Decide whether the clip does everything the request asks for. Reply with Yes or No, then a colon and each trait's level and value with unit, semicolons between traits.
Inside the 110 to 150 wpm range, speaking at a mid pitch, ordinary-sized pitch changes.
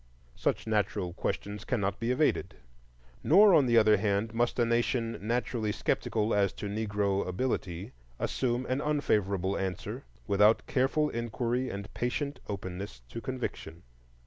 No: slow, 135 wpm; low, 110 Hz; average, 3.8 semitones